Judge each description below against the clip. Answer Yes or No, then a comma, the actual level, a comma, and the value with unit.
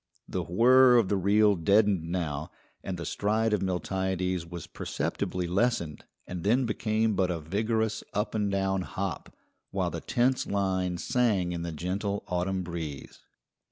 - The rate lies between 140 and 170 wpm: Yes, average, 155 wpm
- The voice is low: Yes, very low, 95 Hz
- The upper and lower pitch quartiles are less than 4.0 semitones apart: Yes, average, 3.4 semitones